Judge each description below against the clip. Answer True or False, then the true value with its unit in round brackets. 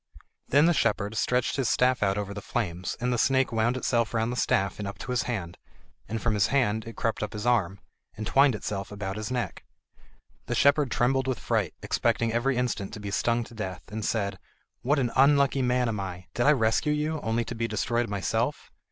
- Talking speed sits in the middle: False (215 wpm)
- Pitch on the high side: False (115 Hz)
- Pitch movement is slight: False (3.6 semitones)